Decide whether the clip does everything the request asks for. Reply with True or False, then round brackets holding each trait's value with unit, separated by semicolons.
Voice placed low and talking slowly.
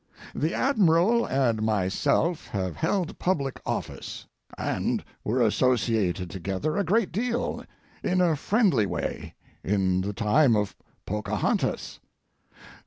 True (130 Hz; 110 wpm)